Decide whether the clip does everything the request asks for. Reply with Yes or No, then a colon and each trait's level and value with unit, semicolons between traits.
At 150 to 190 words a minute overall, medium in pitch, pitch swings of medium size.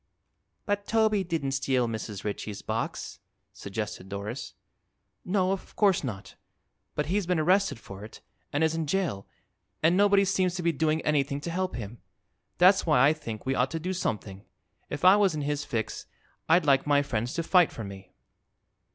No: average, 175 wpm; medium, 150 Hz; wide, 8.1 semitones